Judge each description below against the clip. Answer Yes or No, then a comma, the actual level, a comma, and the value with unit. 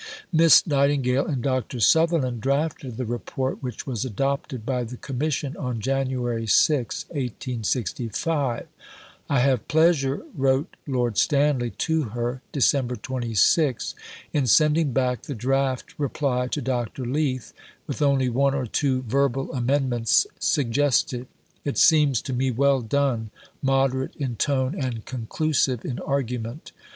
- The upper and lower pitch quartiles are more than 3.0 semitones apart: No, narrow, 2.4 semitones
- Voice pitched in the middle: No, low, 130 Hz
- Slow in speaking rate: Yes, slow, 130 wpm